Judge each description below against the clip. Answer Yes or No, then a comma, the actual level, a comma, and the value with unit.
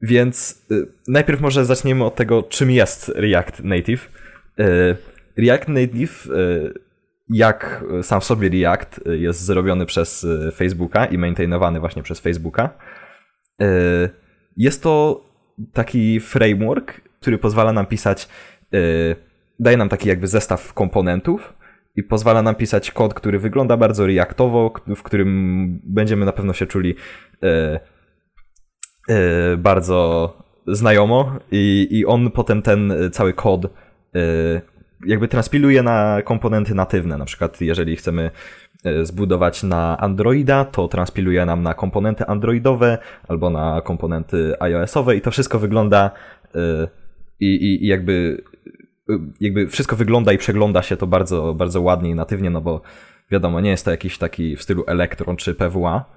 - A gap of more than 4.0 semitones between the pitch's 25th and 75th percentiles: Yes, average, 4.5 semitones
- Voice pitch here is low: Yes, low, 100 Hz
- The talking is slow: No, average, 130 wpm